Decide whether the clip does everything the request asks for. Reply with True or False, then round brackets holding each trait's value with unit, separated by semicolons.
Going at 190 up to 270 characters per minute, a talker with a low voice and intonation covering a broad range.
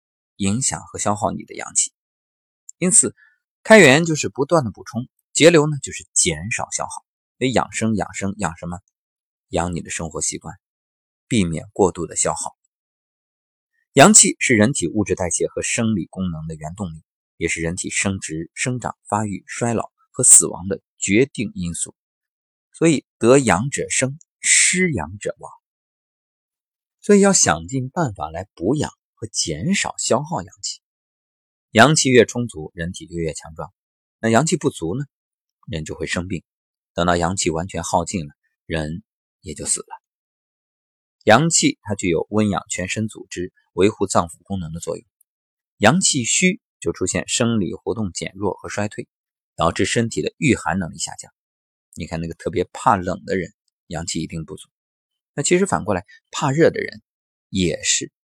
True (235 characters per minute; 100 Hz; 7.8 semitones)